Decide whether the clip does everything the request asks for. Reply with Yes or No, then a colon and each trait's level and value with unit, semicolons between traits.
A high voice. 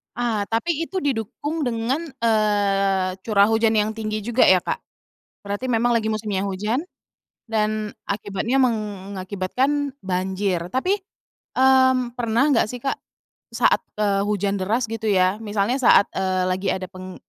Yes: high, 215 Hz